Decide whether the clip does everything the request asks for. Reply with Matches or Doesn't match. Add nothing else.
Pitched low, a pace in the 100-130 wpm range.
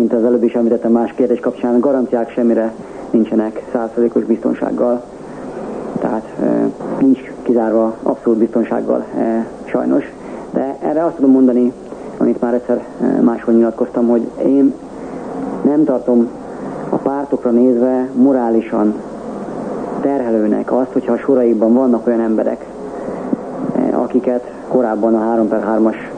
Matches